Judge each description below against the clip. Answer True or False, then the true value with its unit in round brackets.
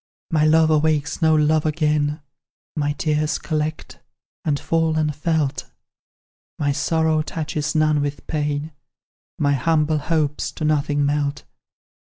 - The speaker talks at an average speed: False (120 wpm)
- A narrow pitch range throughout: True (1.2 semitones)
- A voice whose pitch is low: False (155 Hz)